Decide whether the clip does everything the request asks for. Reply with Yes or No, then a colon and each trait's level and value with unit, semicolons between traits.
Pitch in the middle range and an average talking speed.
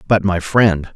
No: very low, 95 Hz; average, 190 wpm